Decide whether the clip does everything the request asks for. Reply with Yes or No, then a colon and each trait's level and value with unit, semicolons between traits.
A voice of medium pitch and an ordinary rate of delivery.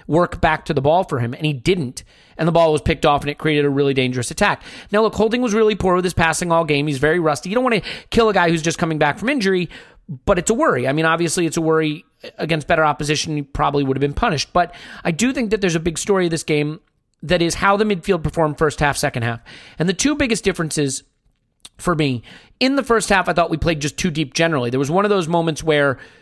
No: medium, 165 Hz; fast, 270 wpm